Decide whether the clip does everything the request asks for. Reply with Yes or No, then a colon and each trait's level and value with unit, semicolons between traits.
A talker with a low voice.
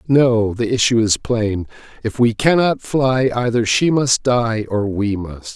Yes: low, 115 Hz